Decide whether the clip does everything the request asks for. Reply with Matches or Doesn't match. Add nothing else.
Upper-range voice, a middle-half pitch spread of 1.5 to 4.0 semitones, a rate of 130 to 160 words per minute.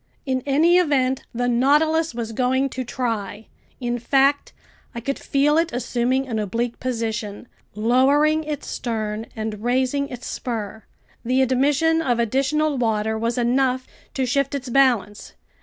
Matches